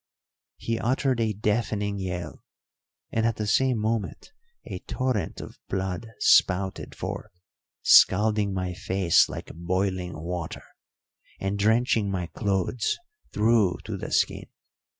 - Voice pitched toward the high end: No, low, 100 Hz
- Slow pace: Yes, slow, 120 wpm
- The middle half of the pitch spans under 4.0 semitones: Yes, average, 3.3 semitones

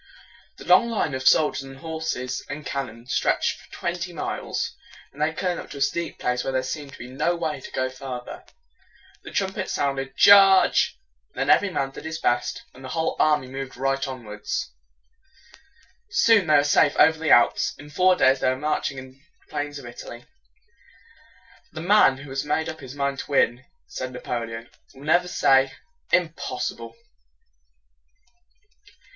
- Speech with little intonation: No, average, 3.6 semitones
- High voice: No, medium, 140 Hz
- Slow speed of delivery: No, average, 175 wpm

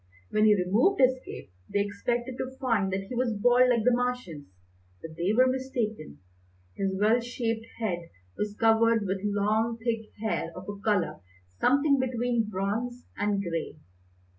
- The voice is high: Yes, high, 225 Hz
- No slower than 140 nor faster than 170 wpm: Yes, average, 160 wpm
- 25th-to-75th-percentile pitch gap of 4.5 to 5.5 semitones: No, average, 3.4 semitones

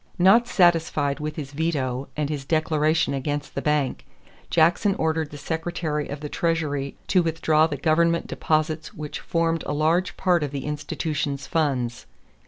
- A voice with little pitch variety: Yes, narrow, 2.2 semitones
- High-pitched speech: No, medium, 155 Hz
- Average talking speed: Yes, average, 155 wpm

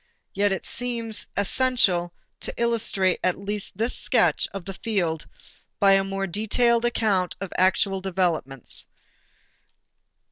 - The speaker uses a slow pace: Yes, slow, 120 wpm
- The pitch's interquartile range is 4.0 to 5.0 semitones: No, average, 3.4 semitones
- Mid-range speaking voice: No, high, 195 Hz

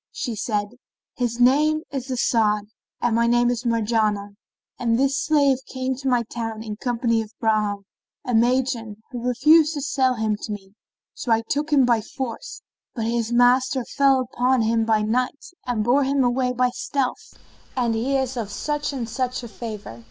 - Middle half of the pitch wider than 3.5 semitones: No, average, 2.9 semitones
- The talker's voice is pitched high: Yes, high, 245 Hz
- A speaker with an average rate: Yes, average, 180 wpm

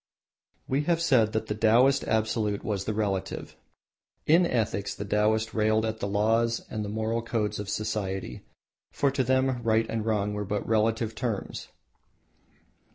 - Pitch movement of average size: No, narrow, 1.8 semitones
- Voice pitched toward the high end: No, low, 110 Hz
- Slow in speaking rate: No, average, 160 wpm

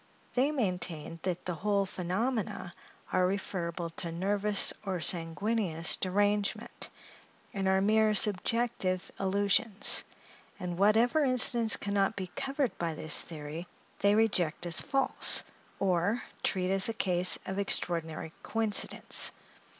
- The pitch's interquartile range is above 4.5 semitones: No, average, 3.4 semitones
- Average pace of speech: No, slow, 120 wpm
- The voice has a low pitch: No, high, 195 Hz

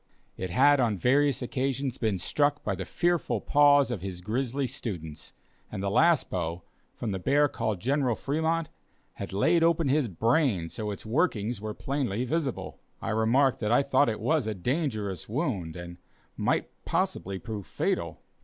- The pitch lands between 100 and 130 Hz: Yes, low, 120 Hz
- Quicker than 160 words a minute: Yes, average, 170 wpm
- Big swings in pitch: Yes, wide, 6.2 semitones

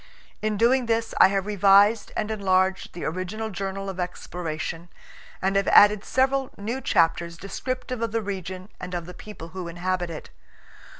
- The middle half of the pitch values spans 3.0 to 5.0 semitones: Yes, average, 3.3 semitones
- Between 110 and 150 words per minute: No, average, 165 wpm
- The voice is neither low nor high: No, high, 195 Hz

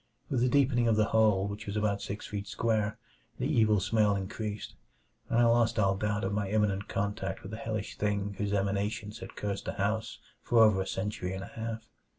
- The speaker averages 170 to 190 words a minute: No, fast, 205 wpm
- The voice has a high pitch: No, low, 105 Hz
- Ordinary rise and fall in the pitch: No, narrow, 1.8 semitones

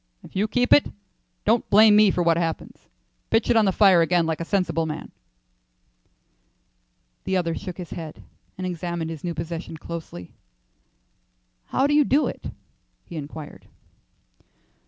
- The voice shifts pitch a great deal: No, average, 4.1 semitones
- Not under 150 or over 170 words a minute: Yes, average, 155 wpm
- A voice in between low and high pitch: Yes, medium, 175 Hz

